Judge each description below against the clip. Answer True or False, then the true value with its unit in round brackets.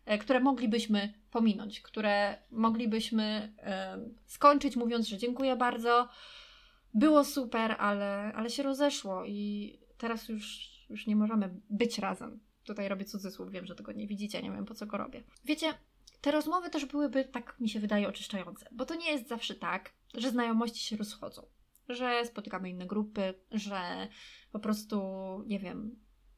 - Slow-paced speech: False (155 wpm)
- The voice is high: True (220 Hz)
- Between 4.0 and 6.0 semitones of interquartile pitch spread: False (3.0 semitones)